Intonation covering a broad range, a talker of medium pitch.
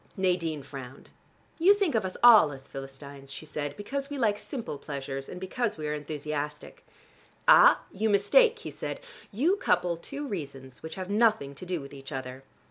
Yes: wide, 7.7 semitones; medium, 165 Hz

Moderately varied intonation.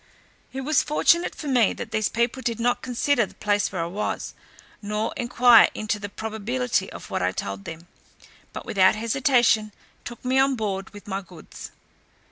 Yes: average, 3.5 semitones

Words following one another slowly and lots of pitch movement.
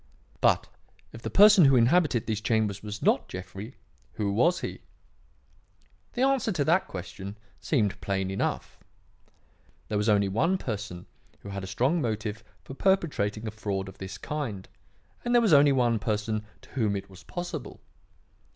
No: average, 160 wpm; wide, 6.7 semitones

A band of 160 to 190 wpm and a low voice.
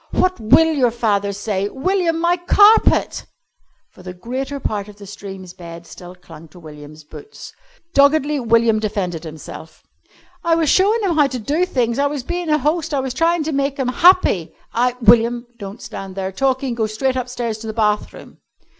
No: average, 185 wpm; high, 240 Hz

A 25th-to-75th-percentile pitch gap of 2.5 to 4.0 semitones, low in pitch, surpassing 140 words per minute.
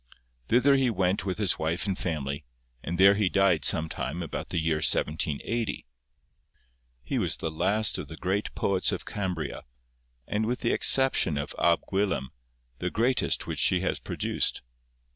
No: average, 4.6 semitones; very low, 95 Hz; average, 160 wpm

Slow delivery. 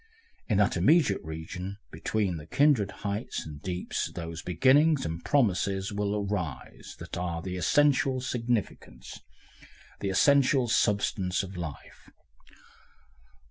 Yes: slow, 115 wpm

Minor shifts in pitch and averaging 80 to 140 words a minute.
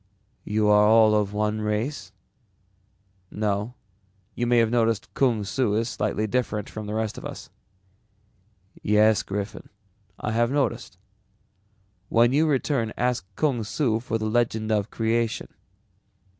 Yes: narrow, 2.2 semitones; slow, 135 wpm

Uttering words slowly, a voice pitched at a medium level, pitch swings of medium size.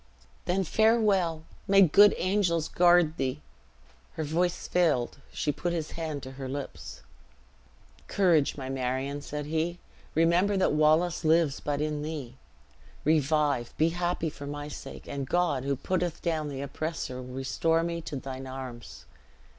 No: average, 145 wpm; medium, 155 Hz; average, 3.8 semitones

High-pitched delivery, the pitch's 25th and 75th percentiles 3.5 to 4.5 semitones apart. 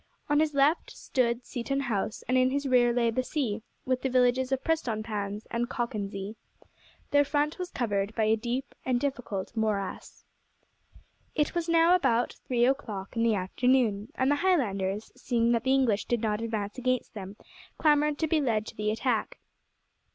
Yes: high, 240 Hz; average, 4.1 semitones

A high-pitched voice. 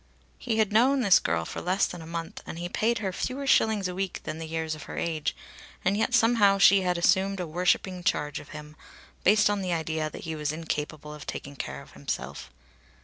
No: medium, 180 Hz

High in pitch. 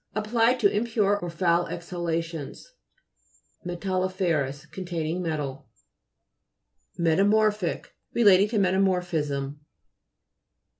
No: medium, 180 Hz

